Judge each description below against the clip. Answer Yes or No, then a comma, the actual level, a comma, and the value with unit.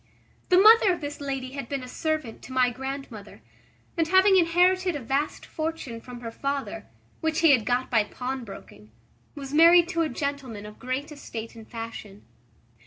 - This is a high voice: Yes, very high, 275 Hz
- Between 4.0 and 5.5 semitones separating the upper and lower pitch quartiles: Yes, average, 5.0 semitones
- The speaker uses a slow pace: No, average, 175 wpm